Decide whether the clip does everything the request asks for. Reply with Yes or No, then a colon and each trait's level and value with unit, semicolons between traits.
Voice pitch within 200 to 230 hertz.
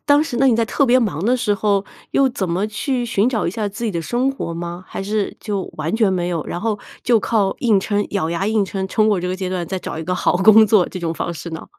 Yes: high, 205 Hz